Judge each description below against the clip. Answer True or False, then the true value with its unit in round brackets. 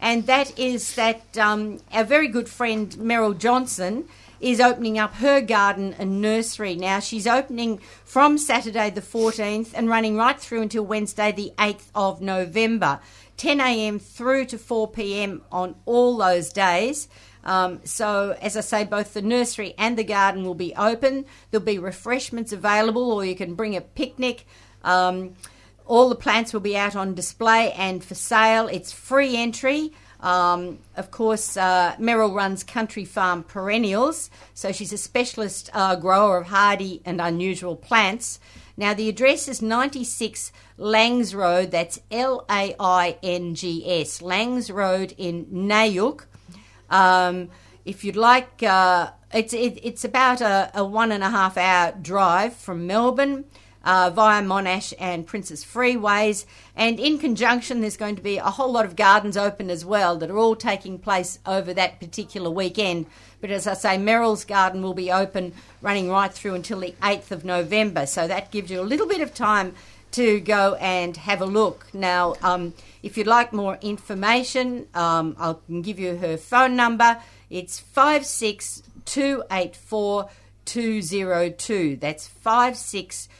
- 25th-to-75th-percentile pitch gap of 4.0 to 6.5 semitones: False (3.6 semitones)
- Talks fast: False (160 wpm)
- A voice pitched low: False (205 Hz)